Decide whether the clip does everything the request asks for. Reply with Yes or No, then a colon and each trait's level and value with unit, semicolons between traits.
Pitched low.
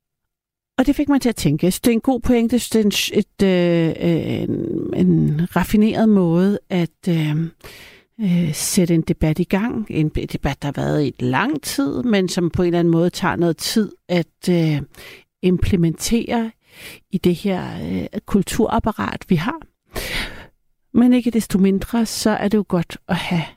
No: medium, 185 Hz